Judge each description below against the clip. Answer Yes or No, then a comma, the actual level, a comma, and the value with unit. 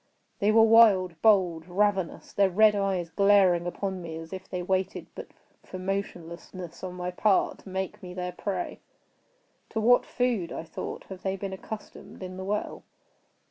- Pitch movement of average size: No, narrow, 2.2 semitones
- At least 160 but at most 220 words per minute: Yes, average, 165 wpm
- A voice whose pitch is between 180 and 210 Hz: Yes, high, 190 Hz